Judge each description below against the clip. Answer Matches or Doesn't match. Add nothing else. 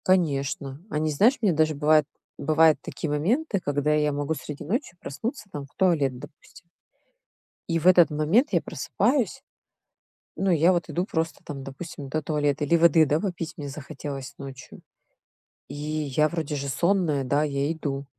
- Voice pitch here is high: Doesn't match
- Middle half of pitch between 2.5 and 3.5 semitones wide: Matches